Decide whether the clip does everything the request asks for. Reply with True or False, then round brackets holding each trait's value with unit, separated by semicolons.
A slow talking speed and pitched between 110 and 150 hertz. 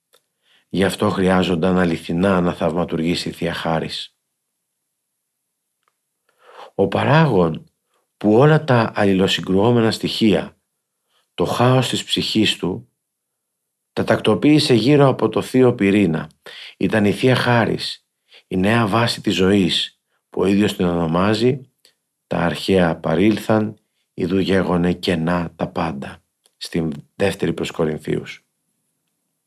False (110 wpm; 100 Hz)